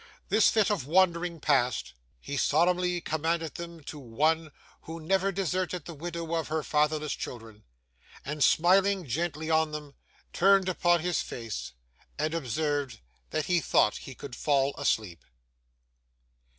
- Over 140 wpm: No, slow, 135 wpm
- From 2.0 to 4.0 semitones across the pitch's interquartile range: Yes, average, 3.3 semitones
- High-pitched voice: No, medium, 160 Hz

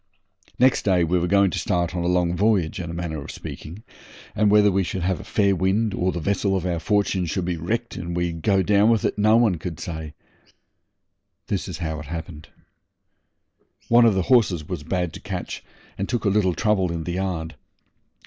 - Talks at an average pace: No, fast, 210 wpm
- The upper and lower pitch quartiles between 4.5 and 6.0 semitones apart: No, average, 3.2 semitones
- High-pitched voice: No, very low, 90 Hz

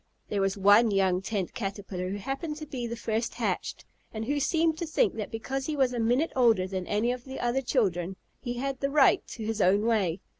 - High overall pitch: Yes, high, 230 Hz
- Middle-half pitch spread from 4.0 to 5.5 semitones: Yes, average, 5.1 semitones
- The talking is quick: Yes, fast, 225 wpm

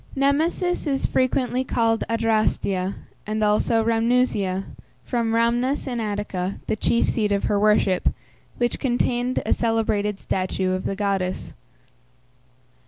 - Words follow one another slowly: Yes, slow, 120 wpm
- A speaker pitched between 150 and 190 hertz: No, high, 225 Hz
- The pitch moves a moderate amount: Yes, average, 3.3 semitones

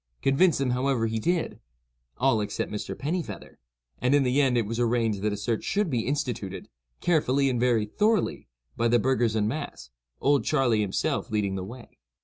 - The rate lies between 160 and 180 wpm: Yes, average, 175 wpm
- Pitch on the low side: Yes, low, 120 Hz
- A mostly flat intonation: No, average, 4.5 semitones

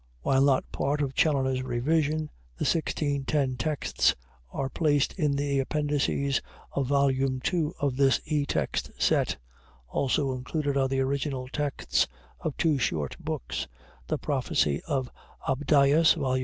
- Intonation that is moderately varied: No, narrow, 2.0 semitones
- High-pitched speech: No, medium, 140 Hz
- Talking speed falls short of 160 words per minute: Yes, slow, 135 wpm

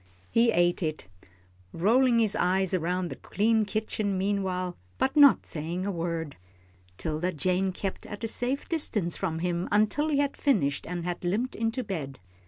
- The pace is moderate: Yes, average, 165 wpm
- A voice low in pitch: No, high, 190 Hz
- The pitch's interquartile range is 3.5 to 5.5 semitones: Yes, average, 4.5 semitones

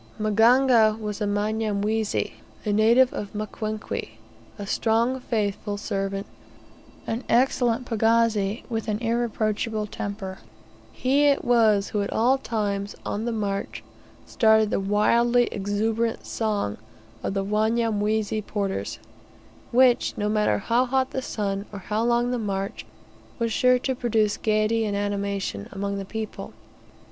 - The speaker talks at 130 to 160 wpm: Yes, slow, 135 wpm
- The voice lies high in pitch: Yes, high, 215 Hz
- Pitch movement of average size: No, narrow, 2.3 semitones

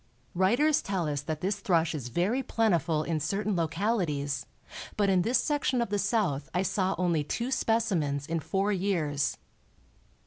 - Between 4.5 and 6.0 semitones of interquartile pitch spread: Yes, average, 5.2 semitones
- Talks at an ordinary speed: Yes, average, 160 wpm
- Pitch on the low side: No, medium, 185 Hz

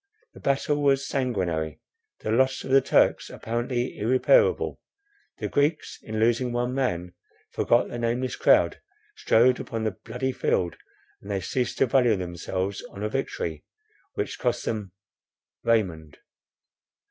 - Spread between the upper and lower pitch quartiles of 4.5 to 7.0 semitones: Yes, average, 5.0 semitones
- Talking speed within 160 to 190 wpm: No, slow, 135 wpm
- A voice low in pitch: Yes, low, 120 Hz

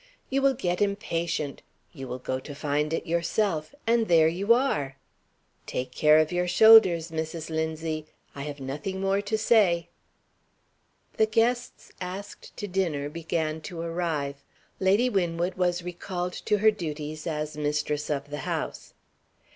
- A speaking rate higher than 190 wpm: No, average, 145 wpm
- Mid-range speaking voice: Yes, medium, 170 Hz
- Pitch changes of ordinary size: Yes, average, 4.3 semitones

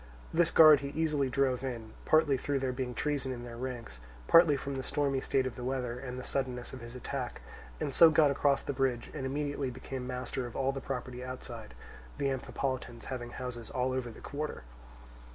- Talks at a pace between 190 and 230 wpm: Yes, average, 200 wpm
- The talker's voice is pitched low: Yes, low, 130 Hz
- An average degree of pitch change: No, narrow, 1.9 semitones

